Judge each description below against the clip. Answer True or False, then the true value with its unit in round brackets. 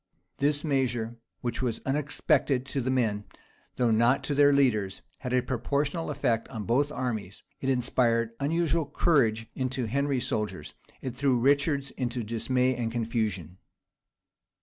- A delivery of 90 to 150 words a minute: True (140 wpm)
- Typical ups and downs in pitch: True (3.5 semitones)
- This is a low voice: True (125 Hz)